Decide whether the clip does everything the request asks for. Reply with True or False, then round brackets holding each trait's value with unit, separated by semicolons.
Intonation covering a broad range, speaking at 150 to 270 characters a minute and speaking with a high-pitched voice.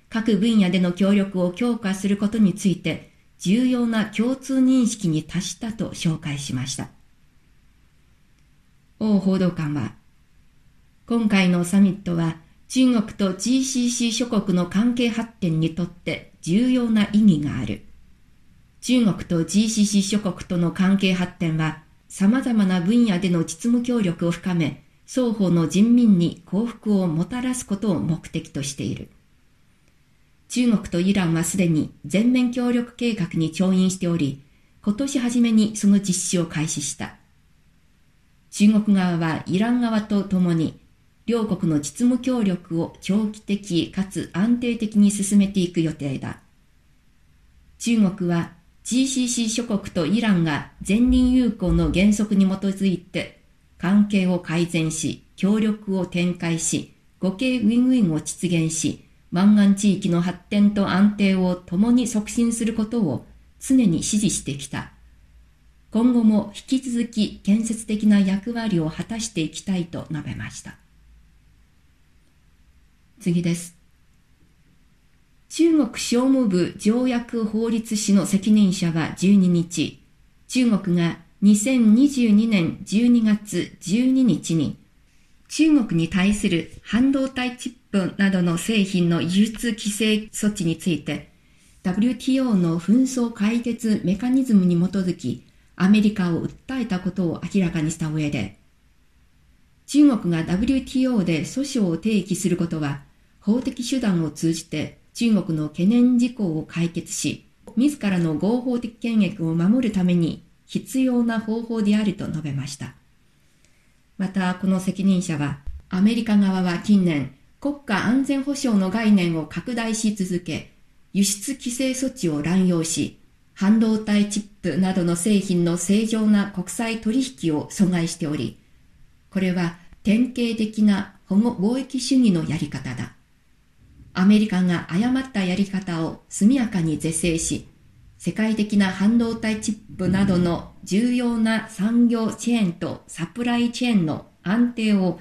False (5.0 semitones; 250 characters per minute; 195 Hz)